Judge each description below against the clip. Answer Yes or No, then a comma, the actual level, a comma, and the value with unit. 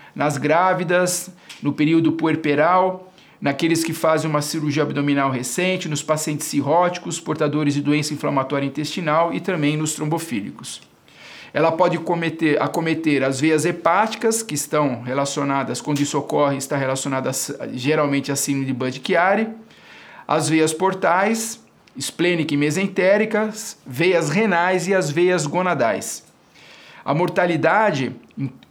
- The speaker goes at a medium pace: No, slow, 120 wpm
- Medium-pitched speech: Yes, medium, 155 Hz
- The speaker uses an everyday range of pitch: Yes, average, 3.7 semitones